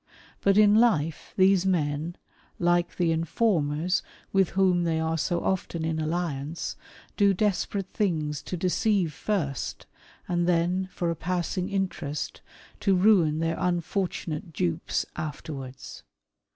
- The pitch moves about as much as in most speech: Yes, average, 3.2 semitones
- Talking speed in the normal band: No, slow, 125 wpm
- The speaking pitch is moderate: Yes, medium, 175 Hz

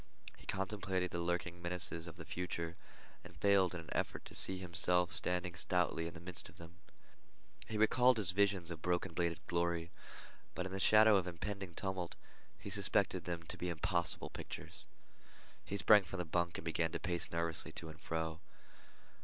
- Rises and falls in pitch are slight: Yes, narrow, 2.1 semitones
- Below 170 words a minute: No, average, 185 wpm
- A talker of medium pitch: No, very low, 90 Hz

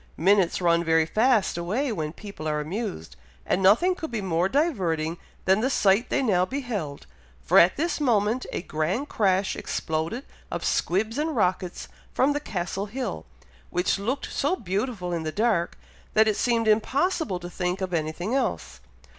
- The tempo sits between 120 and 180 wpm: Yes, average, 165 wpm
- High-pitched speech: Yes, high, 195 Hz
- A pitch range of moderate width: No, wide, 5.8 semitones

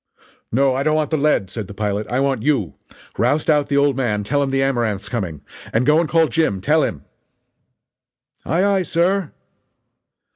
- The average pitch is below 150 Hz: Yes, low, 135 Hz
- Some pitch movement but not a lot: No, wide, 6.1 semitones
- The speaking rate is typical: Yes, average, 185 wpm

